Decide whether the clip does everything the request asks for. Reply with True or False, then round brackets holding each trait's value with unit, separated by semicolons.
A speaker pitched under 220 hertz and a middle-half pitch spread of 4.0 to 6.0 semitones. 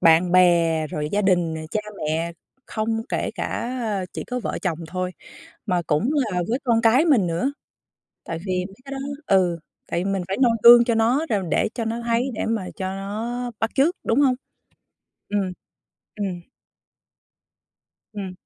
True (205 Hz; 4.8 semitones)